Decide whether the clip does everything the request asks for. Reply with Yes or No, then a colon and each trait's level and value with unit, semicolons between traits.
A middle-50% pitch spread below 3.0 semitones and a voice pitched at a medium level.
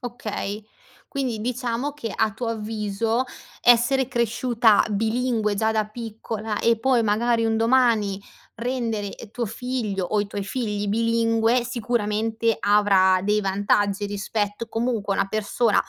No: narrow, 2.4 semitones; high, 225 Hz